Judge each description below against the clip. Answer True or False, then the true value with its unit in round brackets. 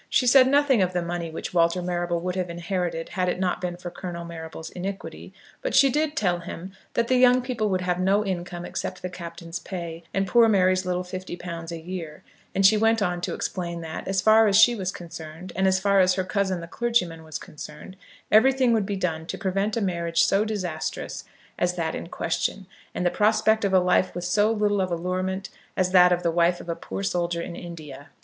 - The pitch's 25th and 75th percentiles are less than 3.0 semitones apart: True (2.6 semitones)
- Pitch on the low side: False (180 Hz)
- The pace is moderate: False (220 wpm)